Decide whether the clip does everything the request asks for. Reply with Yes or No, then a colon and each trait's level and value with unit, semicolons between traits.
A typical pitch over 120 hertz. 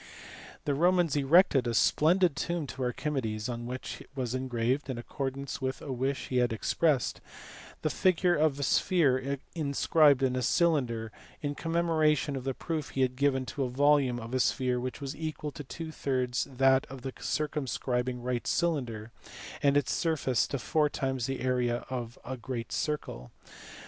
Yes: low, 135 Hz